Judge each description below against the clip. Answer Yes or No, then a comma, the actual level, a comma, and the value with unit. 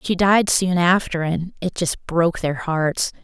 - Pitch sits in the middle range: Yes, medium, 175 Hz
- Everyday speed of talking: Yes, average, 185 wpm